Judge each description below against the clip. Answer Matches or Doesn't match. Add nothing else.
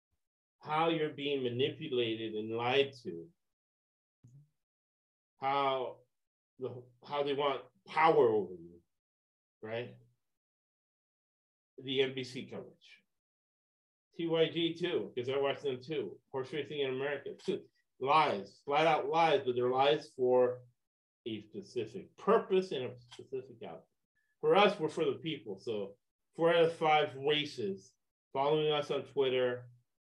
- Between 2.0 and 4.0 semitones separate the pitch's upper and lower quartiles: Doesn't match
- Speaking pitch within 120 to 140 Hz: Matches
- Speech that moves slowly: Matches